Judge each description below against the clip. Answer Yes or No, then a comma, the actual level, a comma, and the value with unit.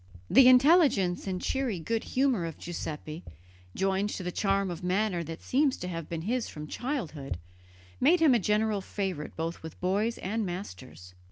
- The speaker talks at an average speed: Yes, average, 175 wpm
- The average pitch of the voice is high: Yes, high, 195 Hz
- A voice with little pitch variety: No, wide, 5.6 semitones